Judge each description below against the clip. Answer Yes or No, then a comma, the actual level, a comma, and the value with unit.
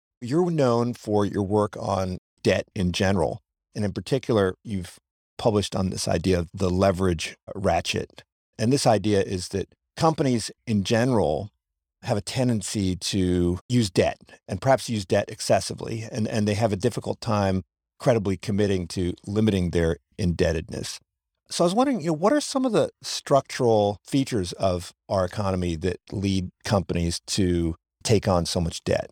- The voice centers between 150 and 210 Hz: No, low, 100 Hz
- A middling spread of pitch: Yes, average, 4.4 semitones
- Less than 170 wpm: Yes, average, 160 wpm